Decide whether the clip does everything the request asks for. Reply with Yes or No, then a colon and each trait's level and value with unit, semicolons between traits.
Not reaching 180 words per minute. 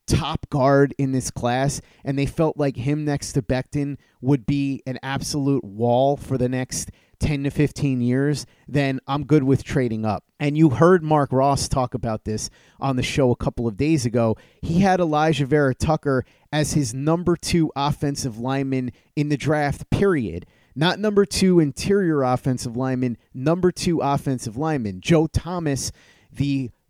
Yes: average, 165 wpm